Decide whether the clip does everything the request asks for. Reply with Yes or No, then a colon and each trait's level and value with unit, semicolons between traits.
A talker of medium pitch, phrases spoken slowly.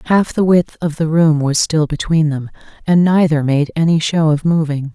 No: medium, 160 Hz; fast, 205 wpm